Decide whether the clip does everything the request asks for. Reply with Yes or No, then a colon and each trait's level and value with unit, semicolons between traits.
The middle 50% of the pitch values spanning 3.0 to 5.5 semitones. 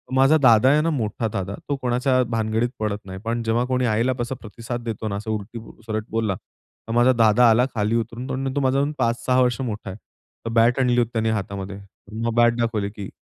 No: narrow, 2.4 semitones